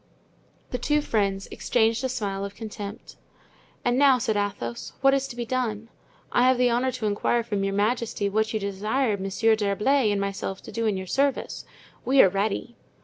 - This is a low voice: No, high, 220 Hz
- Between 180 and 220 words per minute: Yes, average, 190 wpm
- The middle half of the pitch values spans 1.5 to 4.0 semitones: Yes, average, 3.7 semitones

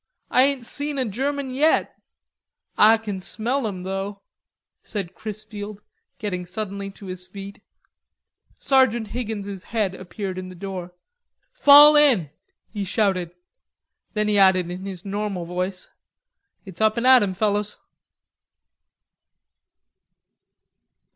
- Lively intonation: No, average, 3.2 semitones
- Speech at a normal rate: No, slow, 120 wpm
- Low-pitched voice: No, high, 205 Hz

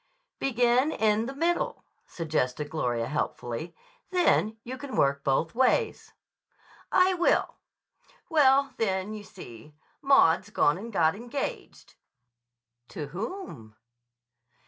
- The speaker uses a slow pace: Yes, slow, 105 wpm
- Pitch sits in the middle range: No, high, 215 Hz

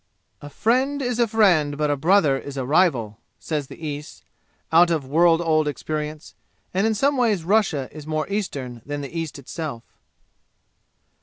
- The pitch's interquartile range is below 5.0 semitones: No, wide, 5.4 semitones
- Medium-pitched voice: Yes, medium, 155 Hz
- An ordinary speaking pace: Yes, average, 165 wpm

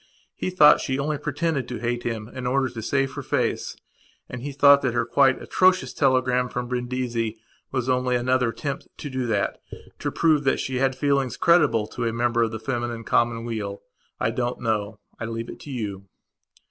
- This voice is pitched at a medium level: No, low, 125 Hz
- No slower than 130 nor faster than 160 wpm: No, average, 185 wpm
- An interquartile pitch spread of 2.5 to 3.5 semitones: Yes, average, 2.8 semitones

